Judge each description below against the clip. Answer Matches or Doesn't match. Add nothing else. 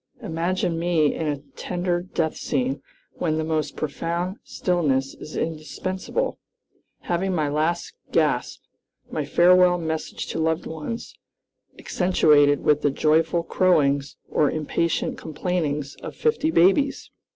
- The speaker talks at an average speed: Doesn't match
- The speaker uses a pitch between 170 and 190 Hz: Doesn't match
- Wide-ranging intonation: Doesn't match